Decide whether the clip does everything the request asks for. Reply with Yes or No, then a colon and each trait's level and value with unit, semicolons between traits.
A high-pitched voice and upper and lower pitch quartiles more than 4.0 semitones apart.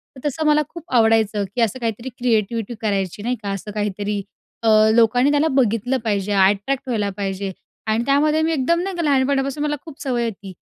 Yes: high, 235 Hz; average, 5.0 semitones